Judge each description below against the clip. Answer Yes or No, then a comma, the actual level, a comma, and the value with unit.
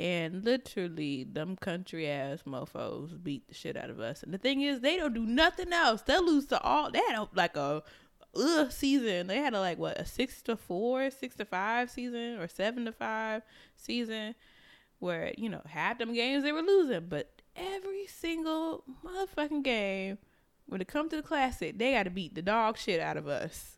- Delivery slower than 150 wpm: No, average, 200 wpm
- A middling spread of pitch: No, wide, 7.4 semitones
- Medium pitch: No, high, 235 Hz